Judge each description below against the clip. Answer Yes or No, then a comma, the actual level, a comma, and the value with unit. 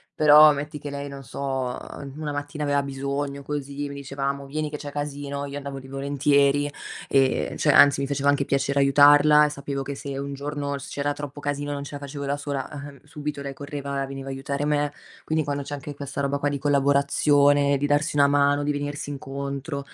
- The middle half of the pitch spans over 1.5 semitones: No, narrow, 0.8 semitones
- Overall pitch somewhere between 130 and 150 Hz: Yes, medium, 140 Hz